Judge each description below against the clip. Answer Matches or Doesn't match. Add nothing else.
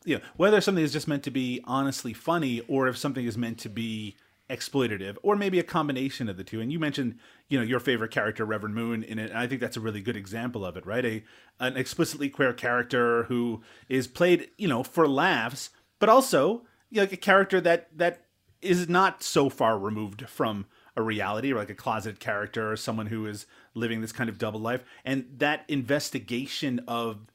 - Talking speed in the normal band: Doesn't match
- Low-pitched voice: Matches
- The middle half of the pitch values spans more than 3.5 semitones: Matches